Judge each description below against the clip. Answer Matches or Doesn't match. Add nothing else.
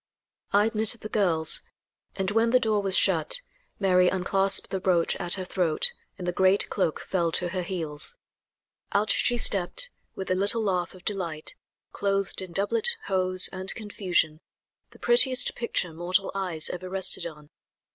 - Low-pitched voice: Doesn't match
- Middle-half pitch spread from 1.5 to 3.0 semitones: Matches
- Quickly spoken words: Doesn't match